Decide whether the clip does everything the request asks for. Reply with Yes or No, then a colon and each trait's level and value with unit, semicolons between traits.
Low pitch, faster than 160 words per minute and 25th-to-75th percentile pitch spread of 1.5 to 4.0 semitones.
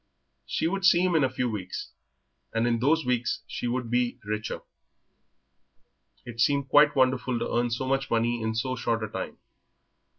Yes: low, 125 Hz; average, 175 wpm; average, 2.7 semitones